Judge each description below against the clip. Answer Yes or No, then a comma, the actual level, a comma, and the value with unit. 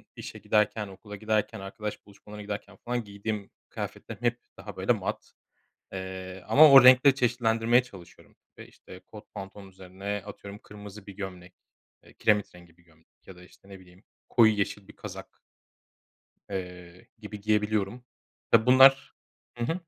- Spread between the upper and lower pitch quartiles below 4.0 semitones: Yes, average, 2.8 semitones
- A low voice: Yes, low, 105 Hz